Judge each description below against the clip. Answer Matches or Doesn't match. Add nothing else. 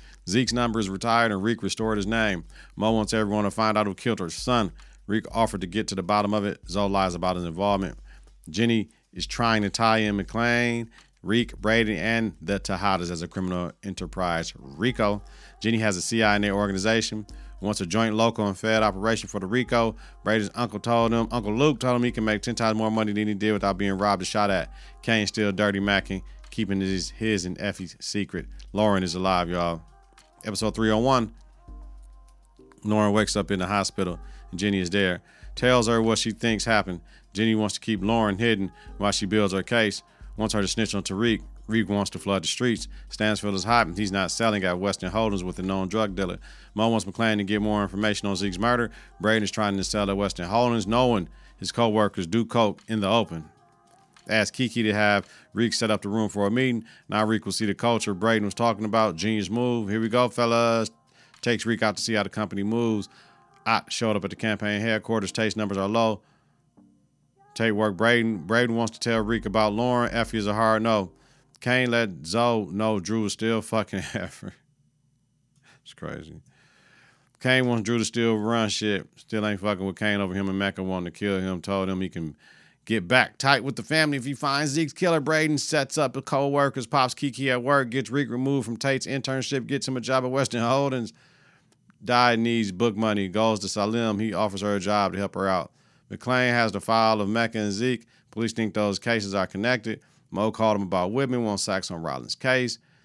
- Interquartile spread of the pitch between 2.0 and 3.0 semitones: Matches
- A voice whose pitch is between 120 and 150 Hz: Doesn't match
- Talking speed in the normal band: Doesn't match